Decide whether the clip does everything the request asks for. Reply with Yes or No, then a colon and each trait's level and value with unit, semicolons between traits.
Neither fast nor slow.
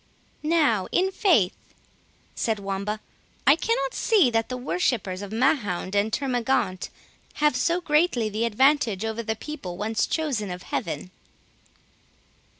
No: slow, 130 wpm